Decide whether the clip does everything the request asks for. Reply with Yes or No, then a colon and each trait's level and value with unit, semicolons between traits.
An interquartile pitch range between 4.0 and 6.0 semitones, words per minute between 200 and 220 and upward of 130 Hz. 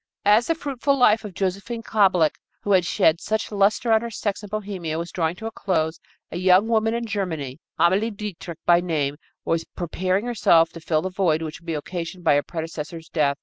Yes: average, 4.5 semitones; fast, 205 wpm; medium, 185 Hz